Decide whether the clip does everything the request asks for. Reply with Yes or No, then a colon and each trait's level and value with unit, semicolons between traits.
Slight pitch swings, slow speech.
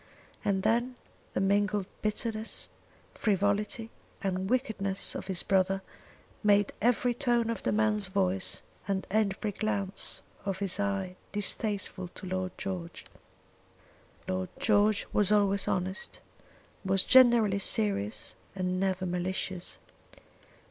Yes: narrow, 2.2 semitones; slow, 115 wpm